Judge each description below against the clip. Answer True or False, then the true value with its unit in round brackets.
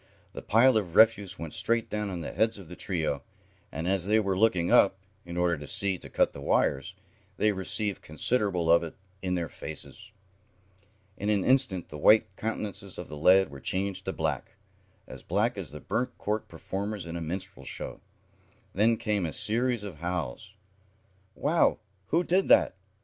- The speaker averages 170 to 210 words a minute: True (180 wpm)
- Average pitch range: True (4.1 semitones)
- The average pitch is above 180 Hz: False (95 Hz)